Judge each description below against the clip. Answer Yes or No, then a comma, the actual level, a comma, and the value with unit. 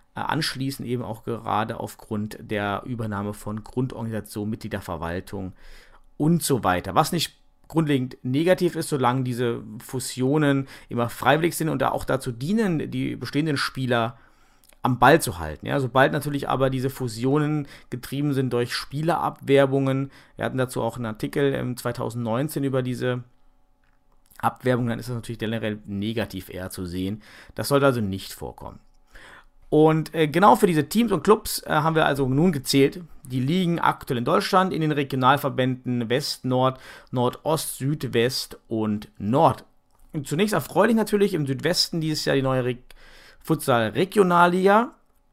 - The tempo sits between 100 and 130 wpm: No, average, 150 wpm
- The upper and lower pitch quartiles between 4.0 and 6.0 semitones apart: Yes, average, 4.5 semitones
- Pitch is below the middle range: Yes, low, 130 Hz